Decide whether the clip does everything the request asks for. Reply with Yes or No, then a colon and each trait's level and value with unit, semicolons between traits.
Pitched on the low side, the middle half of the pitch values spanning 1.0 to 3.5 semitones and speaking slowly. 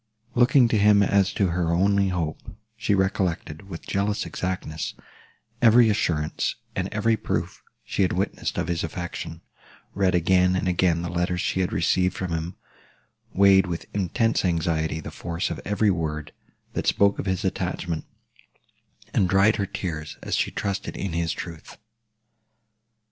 No: very low, 90 Hz; average, 3.0 semitones; average, 155 wpm